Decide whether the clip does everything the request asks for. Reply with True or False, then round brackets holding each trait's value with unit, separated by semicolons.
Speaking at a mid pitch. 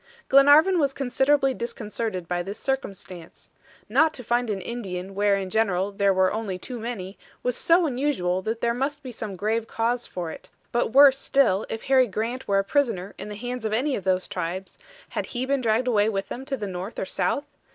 False (225 Hz)